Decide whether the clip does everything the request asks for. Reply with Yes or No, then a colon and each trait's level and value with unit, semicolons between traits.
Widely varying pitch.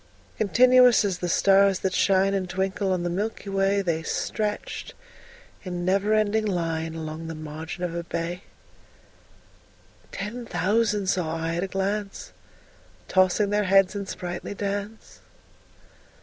No: average, 2.7 semitones